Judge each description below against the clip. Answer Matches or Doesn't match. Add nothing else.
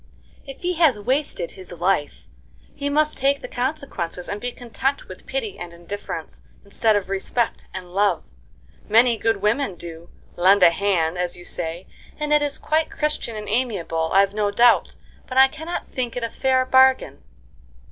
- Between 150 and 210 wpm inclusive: Matches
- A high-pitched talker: Matches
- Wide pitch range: Matches